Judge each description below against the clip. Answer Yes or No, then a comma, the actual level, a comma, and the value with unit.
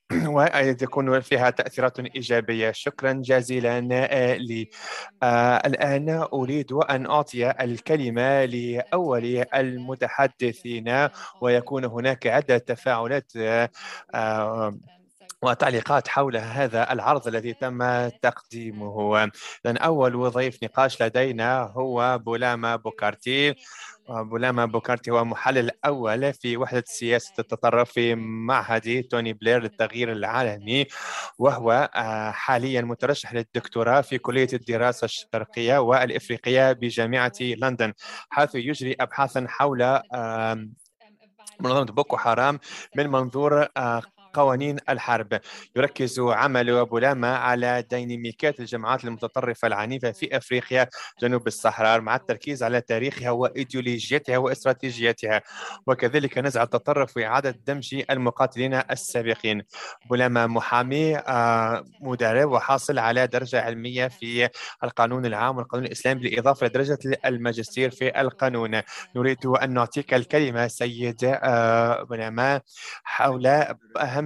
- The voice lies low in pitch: Yes, low, 125 Hz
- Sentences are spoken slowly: Yes, slow, 100 wpm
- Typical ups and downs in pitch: No, narrow, 2.2 semitones